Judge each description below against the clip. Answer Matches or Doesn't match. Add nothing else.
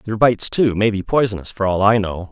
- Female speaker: Doesn't match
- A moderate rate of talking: Doesn't match